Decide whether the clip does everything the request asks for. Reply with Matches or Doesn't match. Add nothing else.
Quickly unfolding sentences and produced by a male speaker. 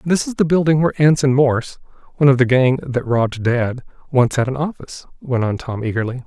Matches